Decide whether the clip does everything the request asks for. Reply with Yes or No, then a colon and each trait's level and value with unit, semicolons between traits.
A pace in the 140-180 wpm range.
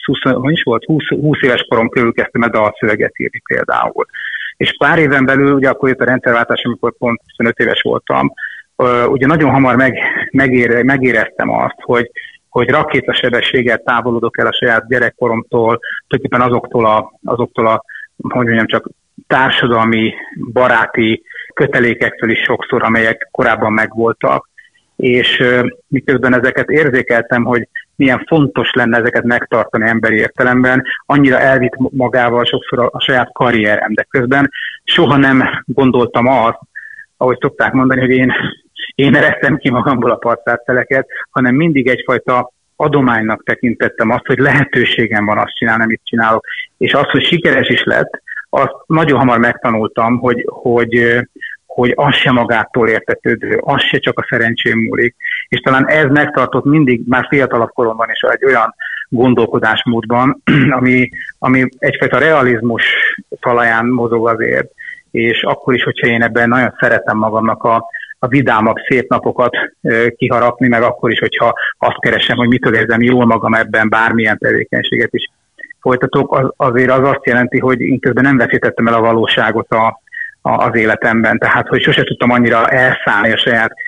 Yes: average, 145 wpm